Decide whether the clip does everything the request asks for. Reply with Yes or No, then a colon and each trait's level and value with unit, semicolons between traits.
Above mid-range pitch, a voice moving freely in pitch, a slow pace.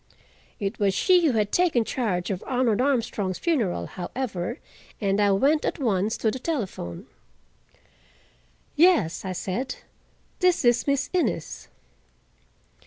Yes: high, 230 Hz; wide, 6.3 semitones; slow, 125 wpm